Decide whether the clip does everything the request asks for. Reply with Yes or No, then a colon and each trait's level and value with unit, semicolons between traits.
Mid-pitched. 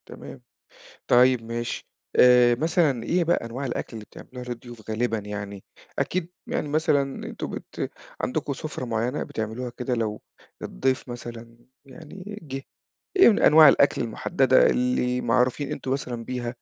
No: low, 125 Hz